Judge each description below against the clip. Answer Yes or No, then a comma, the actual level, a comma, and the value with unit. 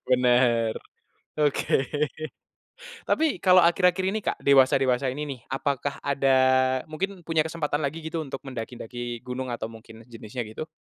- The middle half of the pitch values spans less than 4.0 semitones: No, average, 4.5 semitones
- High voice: No, low, 135 Hz